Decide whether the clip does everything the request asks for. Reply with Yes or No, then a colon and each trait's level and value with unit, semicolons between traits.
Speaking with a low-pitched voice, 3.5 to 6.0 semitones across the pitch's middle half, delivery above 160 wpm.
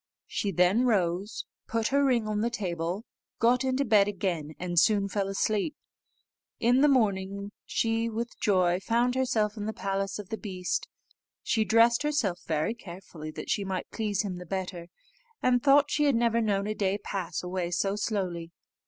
No: high, 205 Hz; average, 3.9 semitones; average, 175 wpm